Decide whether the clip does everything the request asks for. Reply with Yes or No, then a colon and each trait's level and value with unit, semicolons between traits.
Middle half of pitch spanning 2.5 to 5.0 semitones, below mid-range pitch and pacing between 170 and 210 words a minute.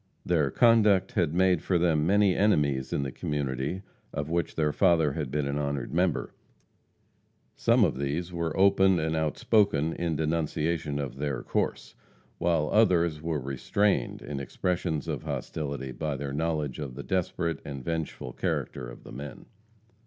No: average, 3.7 semitones; very low, 80 Hz; average, 155 wpm